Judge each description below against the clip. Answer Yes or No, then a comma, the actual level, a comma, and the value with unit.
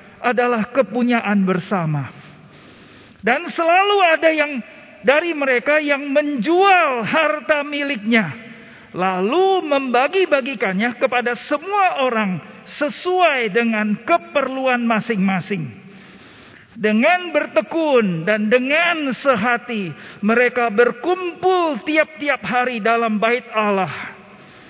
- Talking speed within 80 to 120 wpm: Yes, slow, 85 wpm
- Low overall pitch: No, very high, 250 Hz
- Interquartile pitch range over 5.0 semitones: Yes, wide, 5.4 semitones